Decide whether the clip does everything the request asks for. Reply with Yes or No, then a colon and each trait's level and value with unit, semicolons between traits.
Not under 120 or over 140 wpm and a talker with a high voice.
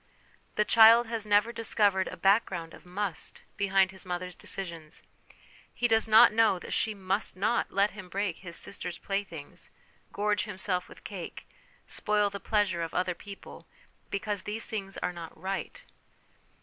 No: average, 155 wpm; high, 195 Hz